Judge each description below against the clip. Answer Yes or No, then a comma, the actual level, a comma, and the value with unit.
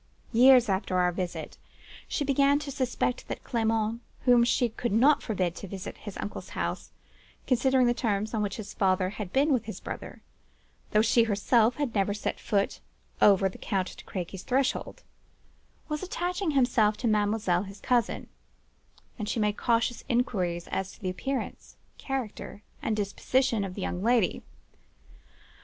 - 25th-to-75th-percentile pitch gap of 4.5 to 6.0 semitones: No, average, 4.0 semitones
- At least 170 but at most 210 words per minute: No, average, 160 wpm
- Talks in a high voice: Yes, high, 220 Hz